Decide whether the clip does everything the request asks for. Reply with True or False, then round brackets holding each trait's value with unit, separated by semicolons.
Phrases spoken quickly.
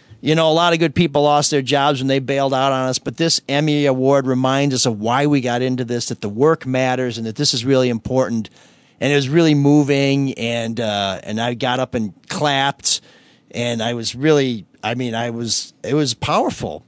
True (220 wpm)